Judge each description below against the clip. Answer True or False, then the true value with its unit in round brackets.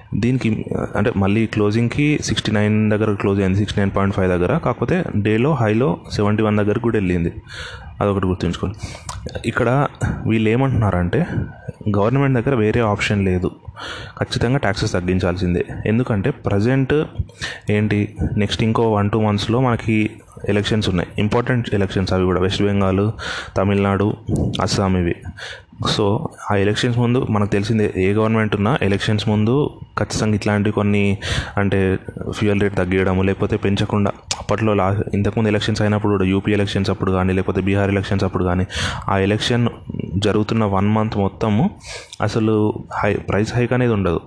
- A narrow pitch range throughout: True (2.3 semitones)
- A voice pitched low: True (105 Hz)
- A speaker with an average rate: False (140 wpm)